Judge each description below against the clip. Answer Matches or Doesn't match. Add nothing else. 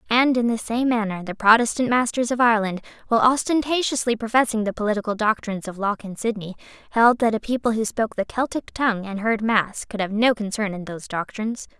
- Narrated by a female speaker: Matches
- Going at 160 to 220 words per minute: Matches